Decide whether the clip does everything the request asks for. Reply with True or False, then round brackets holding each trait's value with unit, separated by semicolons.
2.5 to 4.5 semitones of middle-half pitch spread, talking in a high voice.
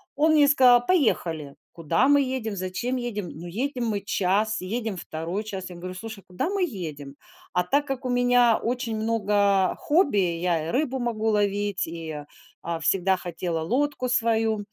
False (5.4 semitones; 215 Hz)